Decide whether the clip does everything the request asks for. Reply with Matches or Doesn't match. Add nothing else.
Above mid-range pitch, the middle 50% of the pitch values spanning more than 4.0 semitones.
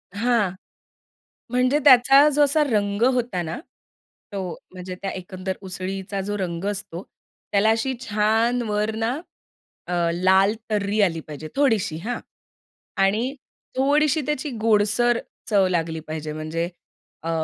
Matches